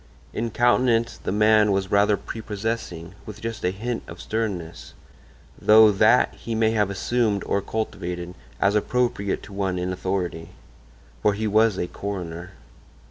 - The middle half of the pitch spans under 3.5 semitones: Yes, average, 2.8 semitones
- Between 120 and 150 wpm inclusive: Yes, average, 145 wpm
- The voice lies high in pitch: No, low, 105 Hz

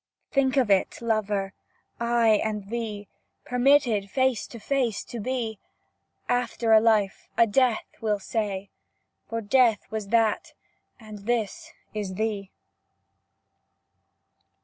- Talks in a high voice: Yes, high, 220 Hz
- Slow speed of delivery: Yes, slow, 115 wpm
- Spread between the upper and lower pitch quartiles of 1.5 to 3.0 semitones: Yes, narrow, 2.5 semitones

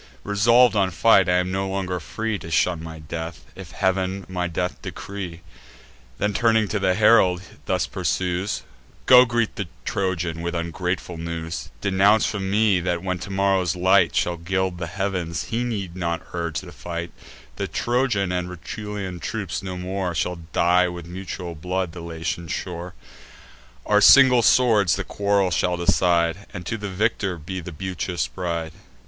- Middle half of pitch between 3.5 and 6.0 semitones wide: No, narrow, 2.5 semitones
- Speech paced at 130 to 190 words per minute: Yes, average, 160 wpm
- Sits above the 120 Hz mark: No, very low, 90 Hz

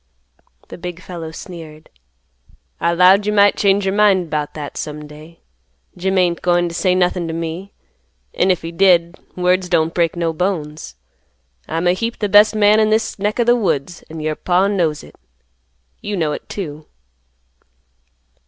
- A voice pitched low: No, medium, 180 Hz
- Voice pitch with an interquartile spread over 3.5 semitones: No, average, 3.2 semitones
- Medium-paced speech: Yes, average, 170 wpm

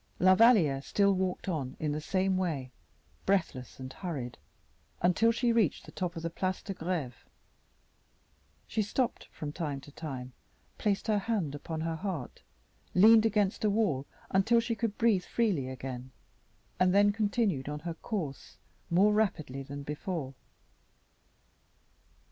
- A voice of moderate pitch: Yes, medium, 180 Hz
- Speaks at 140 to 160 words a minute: Yes, average, 145 wpm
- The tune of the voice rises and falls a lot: Yes, wide, 6.2 semitones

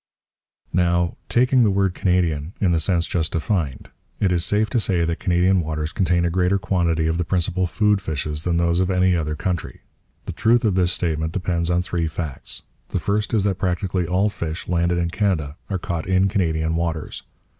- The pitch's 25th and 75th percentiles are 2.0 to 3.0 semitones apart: Yes, narrow, 2.4 semitones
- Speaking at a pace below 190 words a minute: No, average, 195 wpm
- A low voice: Yes, very low, 90 Hz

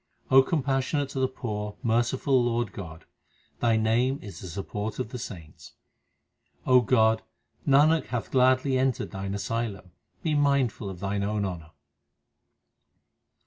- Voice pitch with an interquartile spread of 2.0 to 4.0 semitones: No, average, 4.5 semitones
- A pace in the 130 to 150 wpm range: Yes, slow, 135 wpm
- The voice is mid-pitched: No, low, 115 Hz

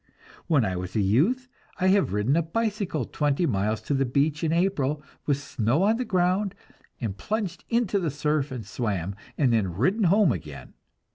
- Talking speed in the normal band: Yes, average, 185 wpm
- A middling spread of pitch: No, wide, 8.9 semitones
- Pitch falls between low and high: Yes, medium, 150 Hz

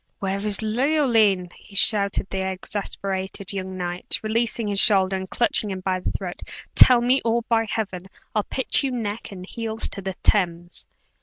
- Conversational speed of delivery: Yes, average, 165 wpm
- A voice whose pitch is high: Yes, high, 200 Hz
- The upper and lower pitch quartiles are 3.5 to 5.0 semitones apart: No, average, 3.1 semitones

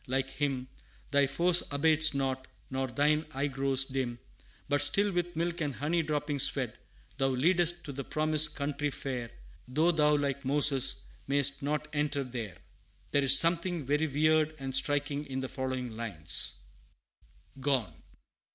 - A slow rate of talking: No, average, 150 wpm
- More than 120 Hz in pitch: Yes, medium, 140 Hz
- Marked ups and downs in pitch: No, narrow, 2.5 semitones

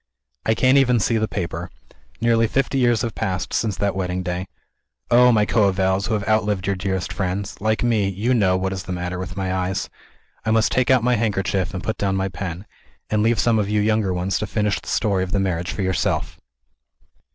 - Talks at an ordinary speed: No, fast, 215 wpm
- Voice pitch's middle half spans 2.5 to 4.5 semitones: Yes, average, 3.0 semitones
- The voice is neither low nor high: No, low, 100 Hz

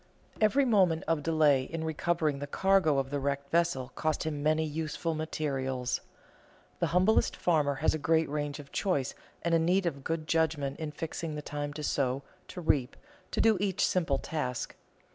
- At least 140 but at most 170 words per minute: No, average, 180 wpm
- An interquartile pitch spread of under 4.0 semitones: Yes, average, 2.7 semitones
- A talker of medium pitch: Yes, medium, 155 Hz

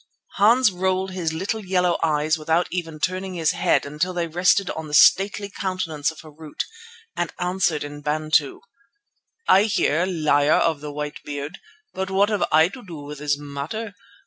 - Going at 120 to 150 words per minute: No, average, 170 wpm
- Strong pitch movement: No, average, 3.9 semitones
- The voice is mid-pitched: Yes, medium, 165 Hz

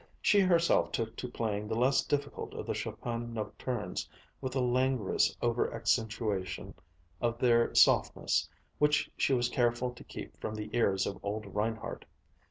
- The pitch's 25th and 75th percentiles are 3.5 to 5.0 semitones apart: No, average, 2.9 semitones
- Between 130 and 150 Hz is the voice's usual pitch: No, low, 115 Hz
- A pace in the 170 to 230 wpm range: No, average, 155 wpm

